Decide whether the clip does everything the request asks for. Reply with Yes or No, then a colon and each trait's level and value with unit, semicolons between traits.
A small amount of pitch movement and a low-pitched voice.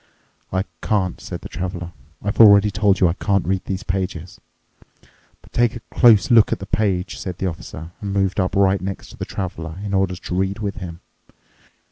Yes: narrow, 1.9 semitones; very low, 95 Hz